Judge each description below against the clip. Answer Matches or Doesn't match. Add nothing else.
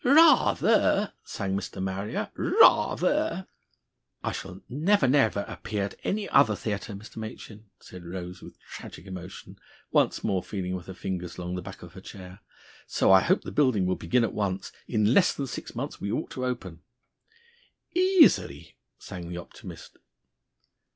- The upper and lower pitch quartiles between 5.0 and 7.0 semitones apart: Matches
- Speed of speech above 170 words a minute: Doesn't match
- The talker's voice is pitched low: Matches